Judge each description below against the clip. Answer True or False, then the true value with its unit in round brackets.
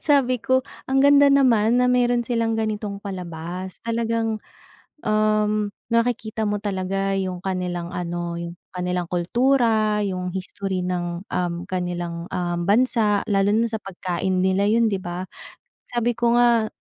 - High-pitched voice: True (205 Hz)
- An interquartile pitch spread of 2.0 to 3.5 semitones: False (4.2 semitones)